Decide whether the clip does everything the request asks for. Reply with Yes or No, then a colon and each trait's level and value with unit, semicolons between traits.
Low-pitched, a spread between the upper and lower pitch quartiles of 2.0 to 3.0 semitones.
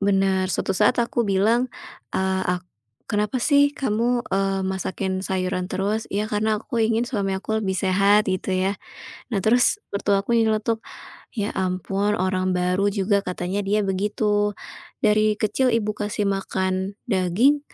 No: high, 205 Hz; narrow, 2.4 semitones